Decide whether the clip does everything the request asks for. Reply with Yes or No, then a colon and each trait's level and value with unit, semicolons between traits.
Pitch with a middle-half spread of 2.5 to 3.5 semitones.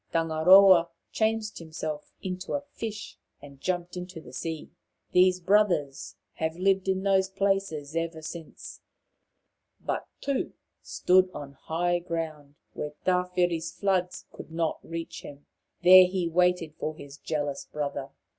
Yes: average, 3.0 semitones